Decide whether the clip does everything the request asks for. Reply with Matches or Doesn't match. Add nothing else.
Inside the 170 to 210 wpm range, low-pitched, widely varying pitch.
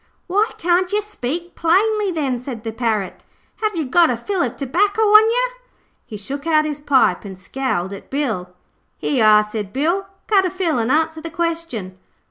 Doesn't match